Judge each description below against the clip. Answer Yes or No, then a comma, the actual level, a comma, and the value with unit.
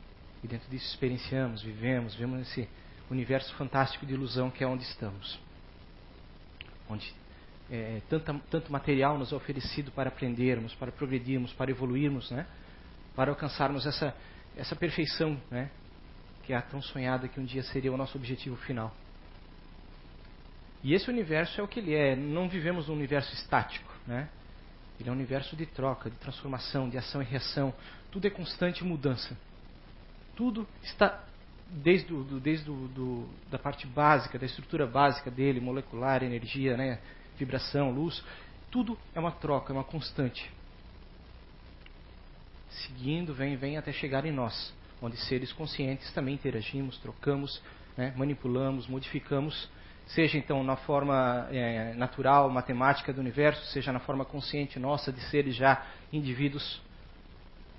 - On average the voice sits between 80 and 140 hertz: Yes, low, 135 Hz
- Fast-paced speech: No, average, 140 wpm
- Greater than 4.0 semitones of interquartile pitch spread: No, average, 2.9 semitones